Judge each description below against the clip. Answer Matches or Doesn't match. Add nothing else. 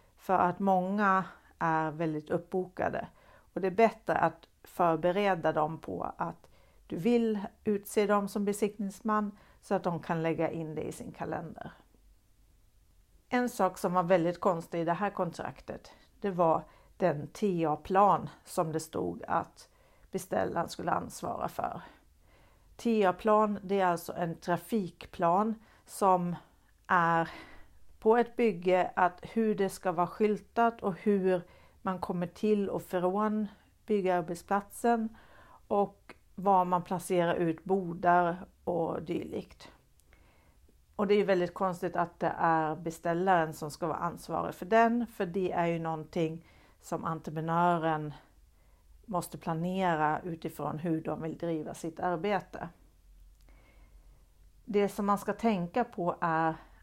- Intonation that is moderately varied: Matches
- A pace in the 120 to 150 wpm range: Matches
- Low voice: Doesn't match